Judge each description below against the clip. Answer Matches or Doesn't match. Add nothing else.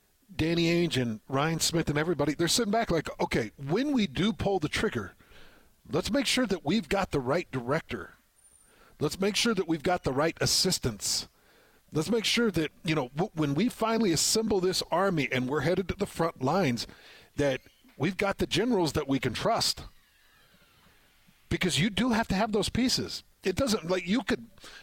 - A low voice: Doesn't match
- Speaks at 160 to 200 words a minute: Matches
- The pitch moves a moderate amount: Doesn't match